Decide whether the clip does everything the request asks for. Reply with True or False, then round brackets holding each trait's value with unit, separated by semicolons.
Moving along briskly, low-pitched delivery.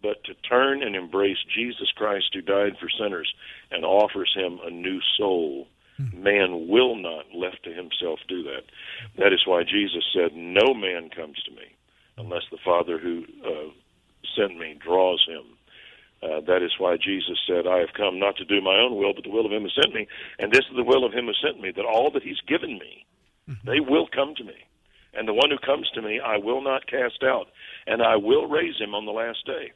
True (220 wpm; 100 Hz)